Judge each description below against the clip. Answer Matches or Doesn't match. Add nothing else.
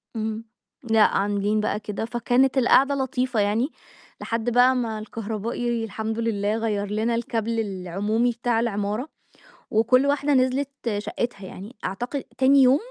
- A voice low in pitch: Doesn't match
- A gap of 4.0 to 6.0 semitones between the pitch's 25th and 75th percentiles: Doesn't match